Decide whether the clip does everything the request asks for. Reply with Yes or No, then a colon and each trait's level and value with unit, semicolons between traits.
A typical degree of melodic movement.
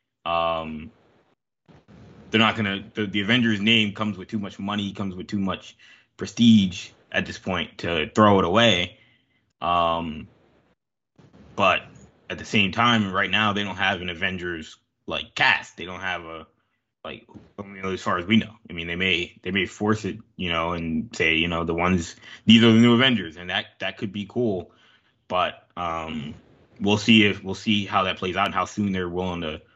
Yes: average, 3.5 semitones